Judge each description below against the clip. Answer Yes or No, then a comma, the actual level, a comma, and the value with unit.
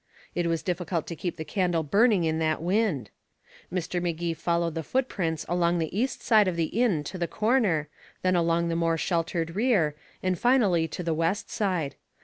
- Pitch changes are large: No, average, 2.8 semitones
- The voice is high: No, medium, 170 Hz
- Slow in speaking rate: No, average, 185 wpm